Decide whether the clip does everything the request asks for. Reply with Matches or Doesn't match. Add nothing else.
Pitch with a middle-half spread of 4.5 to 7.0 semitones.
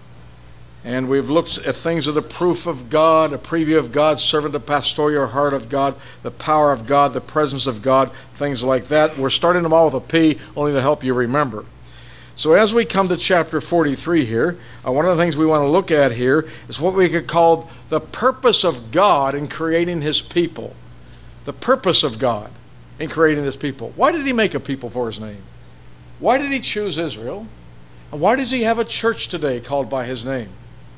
Matches